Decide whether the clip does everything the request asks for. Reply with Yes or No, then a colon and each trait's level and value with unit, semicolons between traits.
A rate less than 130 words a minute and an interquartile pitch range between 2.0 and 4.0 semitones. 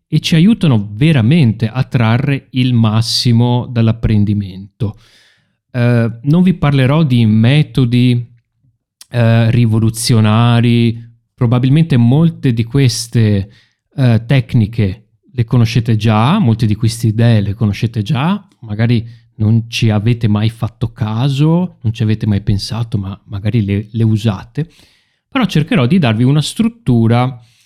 Yes: average, 120 wpm; average, 2.9 semitones